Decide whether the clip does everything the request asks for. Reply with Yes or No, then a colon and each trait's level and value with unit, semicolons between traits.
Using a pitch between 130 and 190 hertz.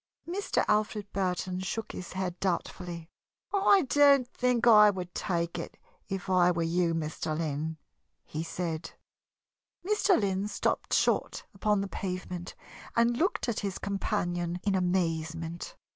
Yes: medium, 185 Hz